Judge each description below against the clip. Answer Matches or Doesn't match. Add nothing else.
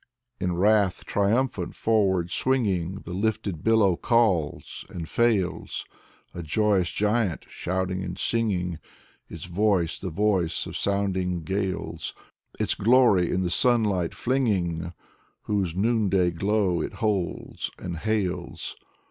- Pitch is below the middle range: Matches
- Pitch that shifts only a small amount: Doesn't match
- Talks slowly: Matches